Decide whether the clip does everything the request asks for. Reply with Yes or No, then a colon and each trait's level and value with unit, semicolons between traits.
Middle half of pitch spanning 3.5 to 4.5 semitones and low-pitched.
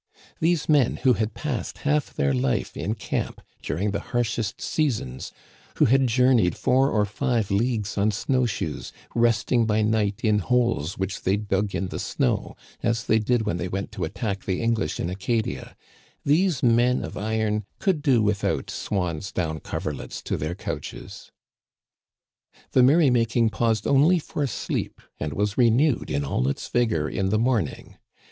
Yes: average, 4.2 semitones; low, 110 Hz